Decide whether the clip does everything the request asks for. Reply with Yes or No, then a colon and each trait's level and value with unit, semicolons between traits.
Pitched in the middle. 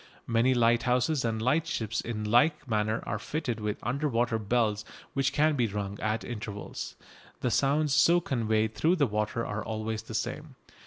No: low, 115 Hz